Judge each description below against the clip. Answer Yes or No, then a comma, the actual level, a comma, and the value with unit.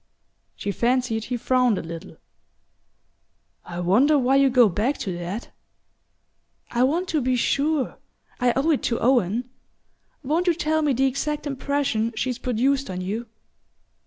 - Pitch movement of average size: Yes, average, 4.0 semitones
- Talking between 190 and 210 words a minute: No, average, 150 wpm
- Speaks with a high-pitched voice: Yes, very high, 255 Hz